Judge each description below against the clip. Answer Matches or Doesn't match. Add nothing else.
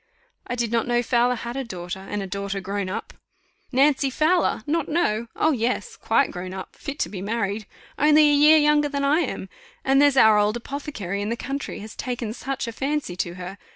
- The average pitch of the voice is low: Doesn't match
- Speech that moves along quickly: Matches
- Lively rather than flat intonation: Matches